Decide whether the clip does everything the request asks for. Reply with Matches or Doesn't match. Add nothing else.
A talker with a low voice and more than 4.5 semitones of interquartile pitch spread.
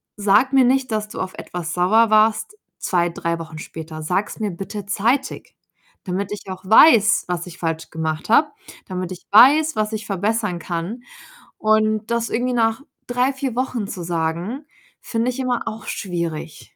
Doesn't match